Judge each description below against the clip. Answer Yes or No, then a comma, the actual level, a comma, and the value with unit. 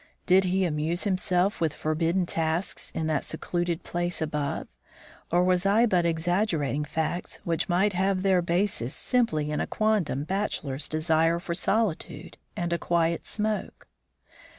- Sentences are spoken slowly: No, average, 145 wpm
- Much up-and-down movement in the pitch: No, average, 3.0 semitones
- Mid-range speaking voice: Yes, medium, 175 Hz